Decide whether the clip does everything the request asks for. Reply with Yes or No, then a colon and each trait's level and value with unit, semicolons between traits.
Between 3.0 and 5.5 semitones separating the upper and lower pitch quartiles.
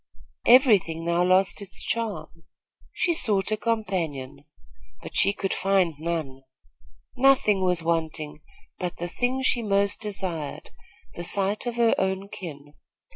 Yes: average, 4.2 semitones